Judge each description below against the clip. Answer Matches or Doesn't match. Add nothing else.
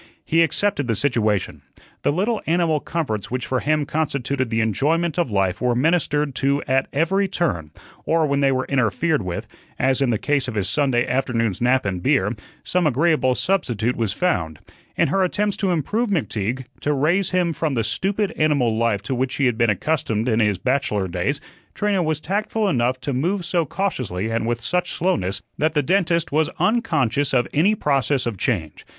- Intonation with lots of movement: Matches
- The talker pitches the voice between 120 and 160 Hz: Matches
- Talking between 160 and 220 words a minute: Matches